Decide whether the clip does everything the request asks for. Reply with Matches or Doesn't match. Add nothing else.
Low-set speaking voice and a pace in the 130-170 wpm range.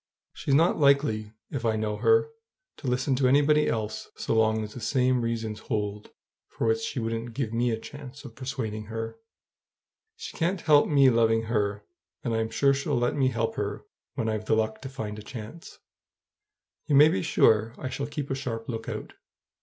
Doesn't match